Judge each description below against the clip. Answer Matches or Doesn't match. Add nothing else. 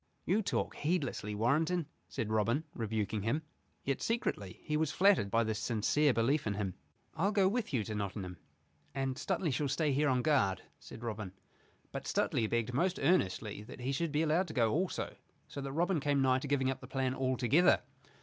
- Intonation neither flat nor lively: Doesn't match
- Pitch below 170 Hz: Matches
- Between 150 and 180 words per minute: Doesn't match